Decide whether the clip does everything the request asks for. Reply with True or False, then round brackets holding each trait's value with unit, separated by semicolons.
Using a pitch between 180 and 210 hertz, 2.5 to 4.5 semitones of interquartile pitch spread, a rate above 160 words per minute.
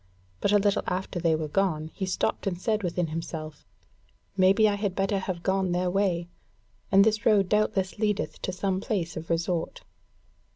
True (190 Hz; 2.8 semitones; 175 wpm)